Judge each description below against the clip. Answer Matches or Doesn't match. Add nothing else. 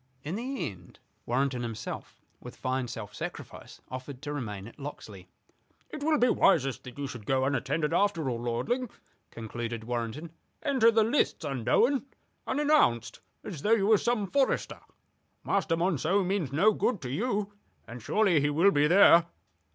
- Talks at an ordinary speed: Matches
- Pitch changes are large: Matches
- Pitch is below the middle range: Doesn't match